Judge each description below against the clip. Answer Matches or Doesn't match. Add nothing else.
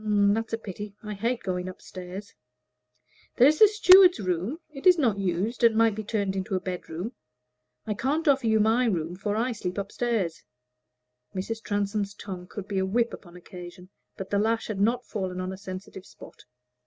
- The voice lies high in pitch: Matches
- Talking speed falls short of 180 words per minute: Doesn't match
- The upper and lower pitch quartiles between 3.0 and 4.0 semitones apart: Matches